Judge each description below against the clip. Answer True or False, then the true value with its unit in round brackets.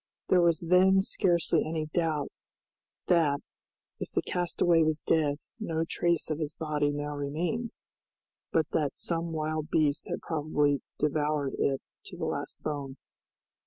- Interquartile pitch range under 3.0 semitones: True (2.4 semitones)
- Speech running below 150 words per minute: True (140 wpm)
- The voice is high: False (155 Hz)